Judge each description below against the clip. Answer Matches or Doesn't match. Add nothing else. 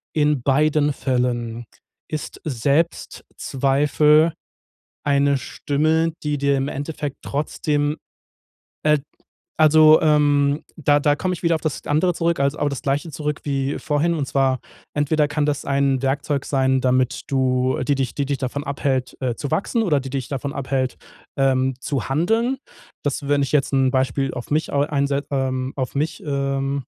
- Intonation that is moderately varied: Doesn't match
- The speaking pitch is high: Doesn't match